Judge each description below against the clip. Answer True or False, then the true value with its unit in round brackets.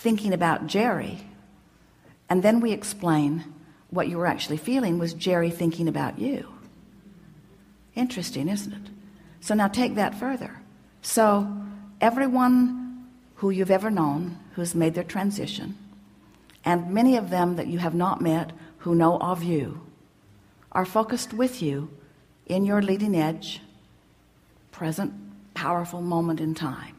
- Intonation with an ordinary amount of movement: True (4.5 semitones)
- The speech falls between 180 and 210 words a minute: False (135 wpm)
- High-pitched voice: False (175 Hz)